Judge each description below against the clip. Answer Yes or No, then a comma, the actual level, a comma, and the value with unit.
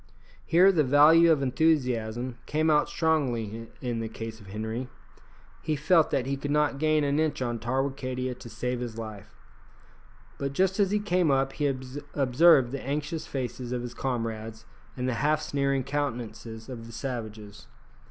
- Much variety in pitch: No, average, 4.1 semitones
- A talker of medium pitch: No, low, 130 Hz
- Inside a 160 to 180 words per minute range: Yes, average, 165 wpm